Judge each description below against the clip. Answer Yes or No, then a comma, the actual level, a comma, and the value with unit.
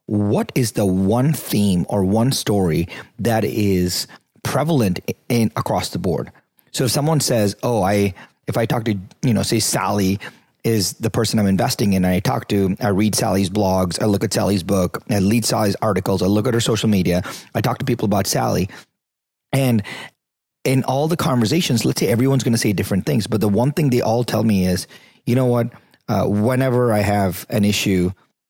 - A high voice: No, low, 110 Hz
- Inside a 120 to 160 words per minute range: No, average, 200 wpm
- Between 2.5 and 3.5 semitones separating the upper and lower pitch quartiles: No, average, 3.9 semitones